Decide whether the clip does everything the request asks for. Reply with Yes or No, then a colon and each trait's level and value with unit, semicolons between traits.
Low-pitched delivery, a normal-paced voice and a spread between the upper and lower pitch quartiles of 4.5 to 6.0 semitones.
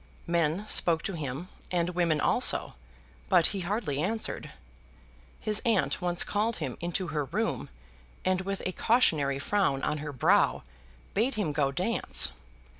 No: medium, 175 Hz; average, 145 wpm; average, 5.1 semitones